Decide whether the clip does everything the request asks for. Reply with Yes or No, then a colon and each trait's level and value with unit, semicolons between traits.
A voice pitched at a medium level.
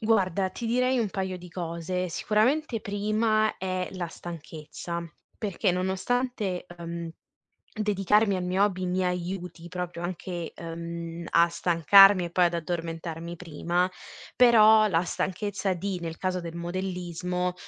Yes: medium, 180 Hz